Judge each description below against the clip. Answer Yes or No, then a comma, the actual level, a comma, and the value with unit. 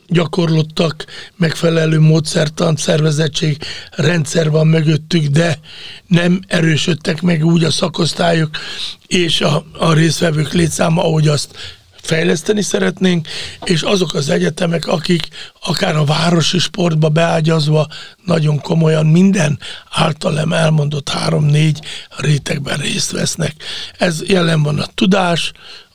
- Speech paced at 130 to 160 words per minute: No, average, 110 wpm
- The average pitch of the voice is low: No, medium, 165 Hz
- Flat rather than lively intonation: Yes, narrow, 2.2 semitones